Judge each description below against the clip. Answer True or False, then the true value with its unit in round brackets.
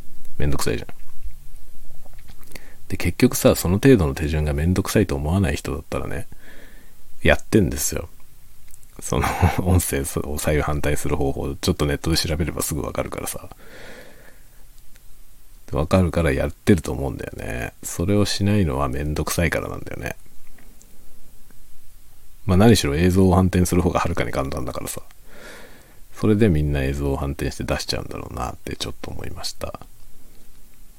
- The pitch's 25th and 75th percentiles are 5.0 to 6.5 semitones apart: True (5.3 semitones)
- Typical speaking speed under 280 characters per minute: False (335 characters per minute)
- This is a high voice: False (85 Hz)